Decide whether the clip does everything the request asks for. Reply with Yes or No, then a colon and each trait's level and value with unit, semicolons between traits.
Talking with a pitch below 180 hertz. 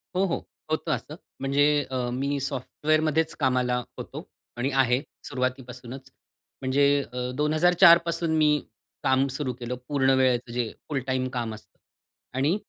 Yes: low, 135 Hz